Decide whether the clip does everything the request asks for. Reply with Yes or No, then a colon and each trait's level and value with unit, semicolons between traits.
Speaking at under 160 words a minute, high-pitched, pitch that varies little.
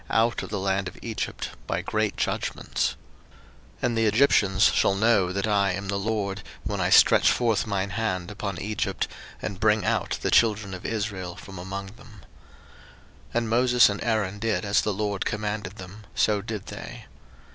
No: average, 145 wpm; low, 105 Hz; narrow, 2.2 semitones